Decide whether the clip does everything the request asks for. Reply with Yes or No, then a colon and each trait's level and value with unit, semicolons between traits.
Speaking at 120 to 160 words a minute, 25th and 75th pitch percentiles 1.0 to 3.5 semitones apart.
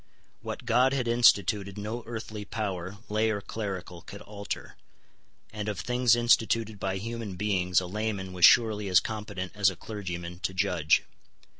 Yes: average, 155 wpm; average, 3.0 semitones